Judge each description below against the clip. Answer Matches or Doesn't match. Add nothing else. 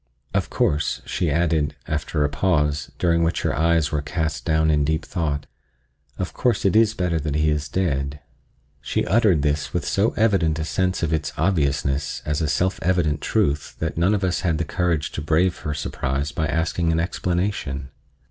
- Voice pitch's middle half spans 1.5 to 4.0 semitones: Matches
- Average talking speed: Matches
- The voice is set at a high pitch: Doesn't match